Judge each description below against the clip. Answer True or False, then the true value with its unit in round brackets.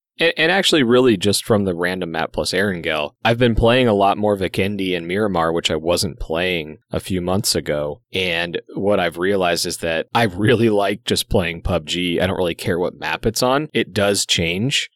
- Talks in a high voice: False (95 Hz)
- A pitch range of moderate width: True (3.9 semitones)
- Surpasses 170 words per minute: True (200 wpm)